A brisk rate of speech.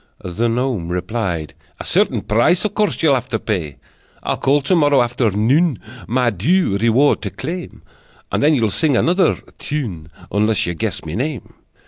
No: average, 165 wpm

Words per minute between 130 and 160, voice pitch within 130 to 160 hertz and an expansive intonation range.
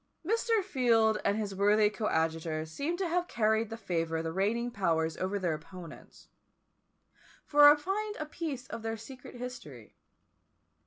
No: average, 155 wpm; high, 220 Hz; wide, 8.4 semitones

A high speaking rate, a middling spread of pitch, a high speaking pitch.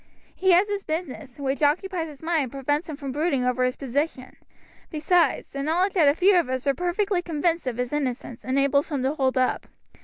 Yes: fast, 210 wpm; average, 4.6 semitones; very high, 290 Hz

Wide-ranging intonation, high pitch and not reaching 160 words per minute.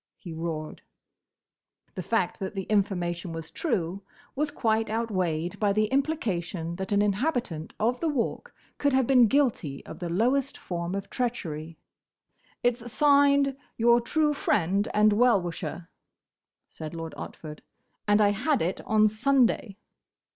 Yes: wide, 6.2 semitones; high, 210 Hz; average, 140 wpm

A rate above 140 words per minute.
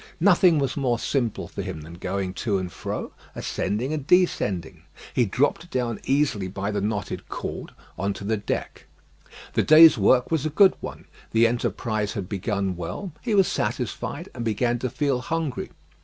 Yes: average, 170 wpm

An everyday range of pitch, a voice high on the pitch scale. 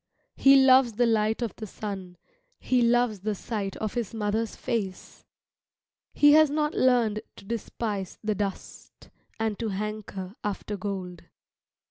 Yes: average, 3.1 semitones; high, 215 Hz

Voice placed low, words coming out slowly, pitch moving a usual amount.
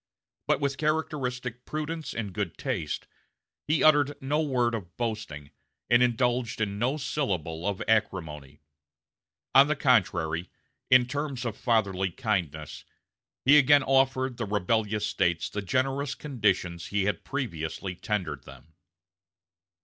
No: low, 115 Hz; slow, 125 wpm; wide, 6.2 semitones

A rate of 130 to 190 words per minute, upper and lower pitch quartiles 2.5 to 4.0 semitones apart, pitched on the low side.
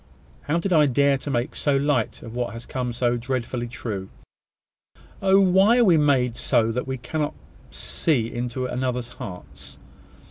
Yes: average, 170 wpm; average, 3.7 semitones; low, 125 Hz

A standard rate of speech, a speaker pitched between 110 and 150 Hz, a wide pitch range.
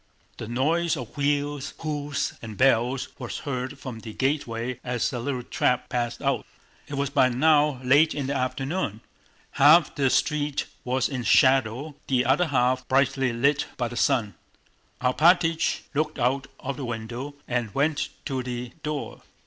No: average, 155 wpm; low, 135 Hz; average, 2.8 semitones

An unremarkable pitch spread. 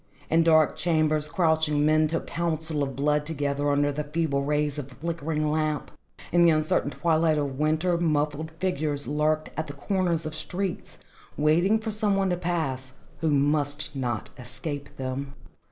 No: narrow, 2.3 semitones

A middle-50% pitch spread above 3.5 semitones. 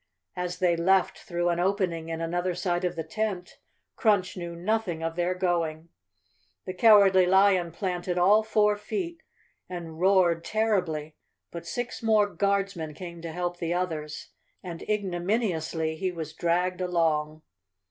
No: average, 2.7 semitones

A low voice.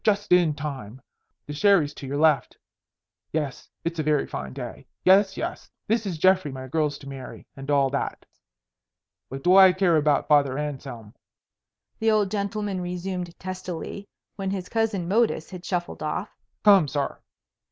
No: medium, 170 Hz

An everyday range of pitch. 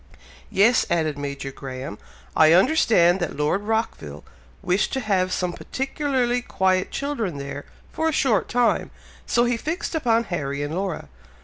No: wide, 7.9 semitones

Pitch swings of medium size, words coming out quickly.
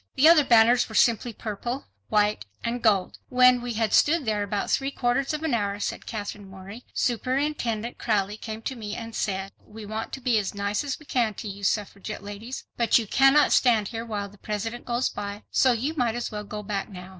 Yes: average, 3.2 semitones; fast, 215 wpm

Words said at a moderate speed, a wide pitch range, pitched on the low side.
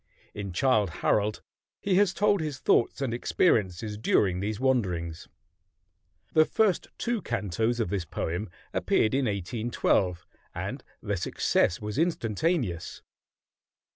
No: slow, 120 wpm; wide, 6.1 semitones; low, 110 Hz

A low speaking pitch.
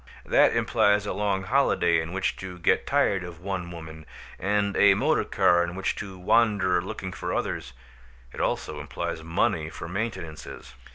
Yes: very low, 95 Hz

